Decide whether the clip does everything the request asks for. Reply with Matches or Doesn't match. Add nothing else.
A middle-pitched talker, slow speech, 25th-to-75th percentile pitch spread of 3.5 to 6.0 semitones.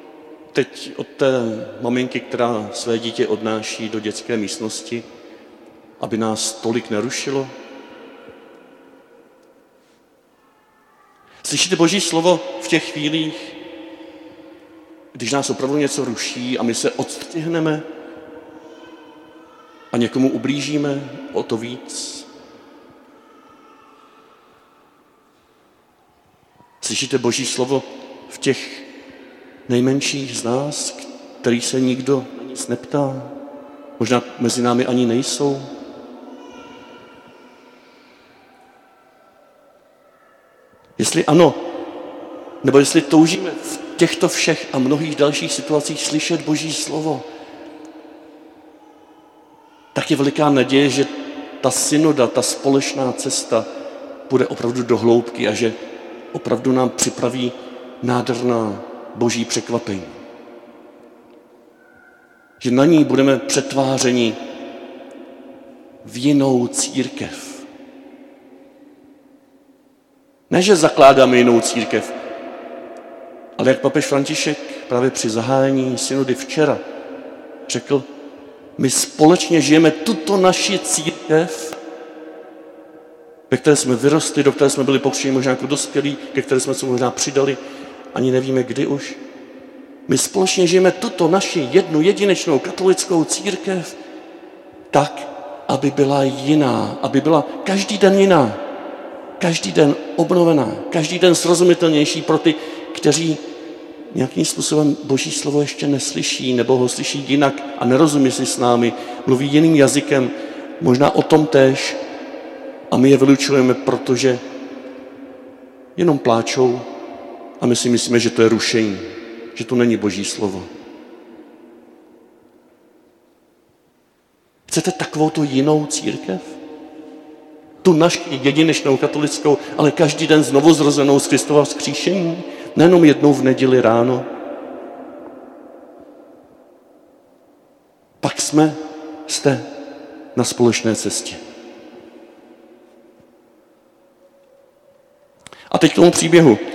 Matches